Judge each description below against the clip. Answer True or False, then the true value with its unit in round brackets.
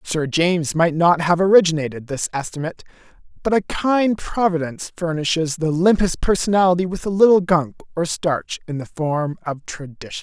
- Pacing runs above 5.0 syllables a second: True (5.3 syllables/s)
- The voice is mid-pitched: True (170 Hz)